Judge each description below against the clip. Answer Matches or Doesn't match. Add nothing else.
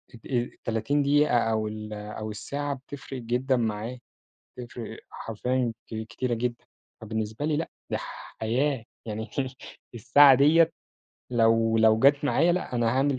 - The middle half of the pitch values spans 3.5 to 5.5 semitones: Matches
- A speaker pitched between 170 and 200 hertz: Doesn't match